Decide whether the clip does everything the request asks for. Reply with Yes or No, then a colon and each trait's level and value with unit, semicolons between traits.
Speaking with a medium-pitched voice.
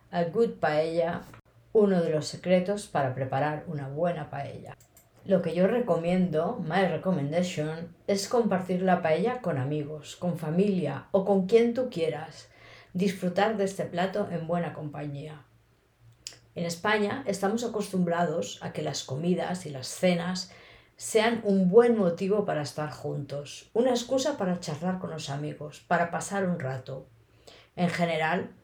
Yes: medium, 170 Hz